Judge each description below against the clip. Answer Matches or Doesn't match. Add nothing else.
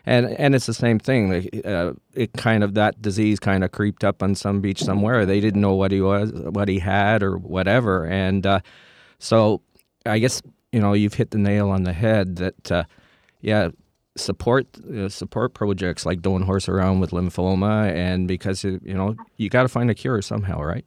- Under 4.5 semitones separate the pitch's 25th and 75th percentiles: Matches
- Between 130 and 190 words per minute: Doesn't match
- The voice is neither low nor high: Doesn't match